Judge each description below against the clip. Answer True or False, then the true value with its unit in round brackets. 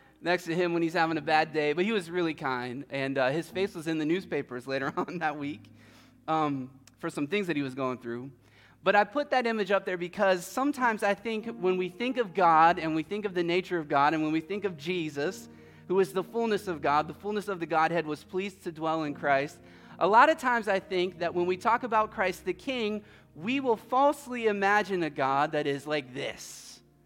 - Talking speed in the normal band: False (235 wpm)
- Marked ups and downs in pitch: True (5.7 semitones)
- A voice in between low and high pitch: True (170 Hz)